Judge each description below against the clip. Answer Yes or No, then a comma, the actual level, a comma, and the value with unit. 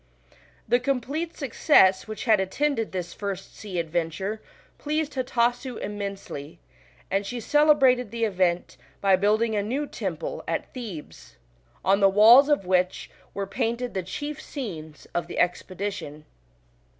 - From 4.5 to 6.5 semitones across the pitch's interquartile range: Yes, average, 5.2 semitones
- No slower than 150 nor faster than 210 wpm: No, slow, 135 wpm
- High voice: Yes, high, 210 Hz